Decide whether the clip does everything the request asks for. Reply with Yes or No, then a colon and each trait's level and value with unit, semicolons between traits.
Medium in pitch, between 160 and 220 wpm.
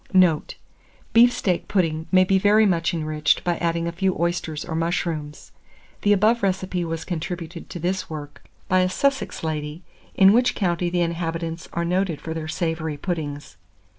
Yes: medium, 170 Hz; average, 165 wpm